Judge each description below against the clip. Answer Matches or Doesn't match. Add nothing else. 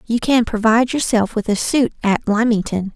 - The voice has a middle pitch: Doesn't match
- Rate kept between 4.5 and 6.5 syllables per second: Matches